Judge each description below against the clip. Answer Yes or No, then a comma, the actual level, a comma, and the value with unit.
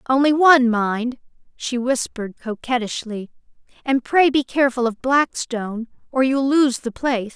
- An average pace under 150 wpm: Yes, average, 140 wpm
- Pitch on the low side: No, very high, 250 Hz